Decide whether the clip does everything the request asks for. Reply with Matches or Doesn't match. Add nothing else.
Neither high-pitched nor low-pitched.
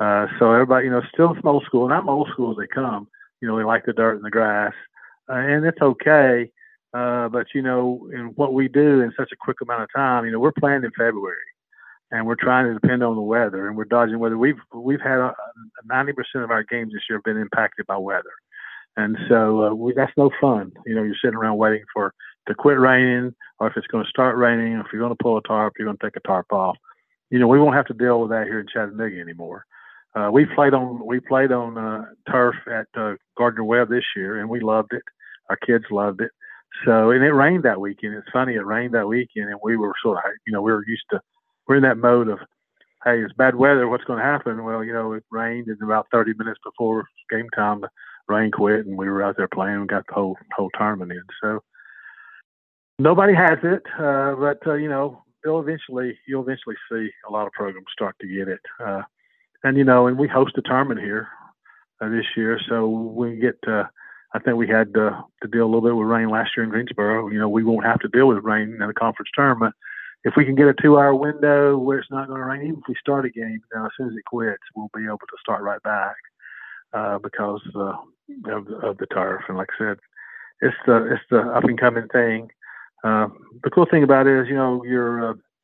Doesn't match